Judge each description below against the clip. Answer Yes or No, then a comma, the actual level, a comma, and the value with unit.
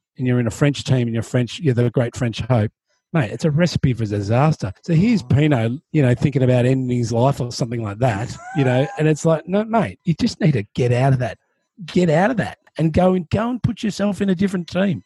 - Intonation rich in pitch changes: Yes, wide, 6.4 semitones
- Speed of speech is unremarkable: No, fast, 255 wpm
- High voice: No, medium, 140 Hz